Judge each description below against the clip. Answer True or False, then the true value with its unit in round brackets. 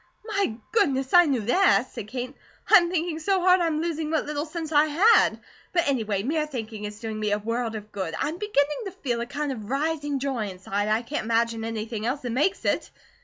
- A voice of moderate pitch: False (275 Hz)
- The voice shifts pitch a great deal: True (6.3 semitones)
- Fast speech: True (225 wpm)